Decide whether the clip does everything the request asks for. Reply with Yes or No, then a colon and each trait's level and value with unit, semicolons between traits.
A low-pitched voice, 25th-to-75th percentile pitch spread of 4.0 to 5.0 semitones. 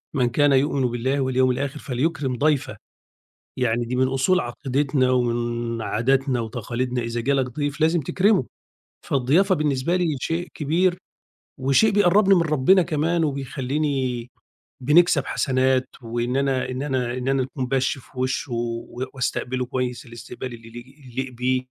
No: low, 130 Hz; average, 2.9 semitones